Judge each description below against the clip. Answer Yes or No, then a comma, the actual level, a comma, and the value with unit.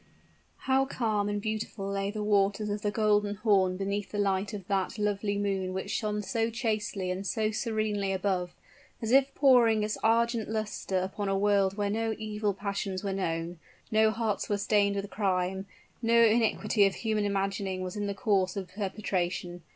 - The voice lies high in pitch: Yes, high, 205 Hz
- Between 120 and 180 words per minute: Yes, average, 175 wpm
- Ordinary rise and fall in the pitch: No, narrow, 1.8 semitones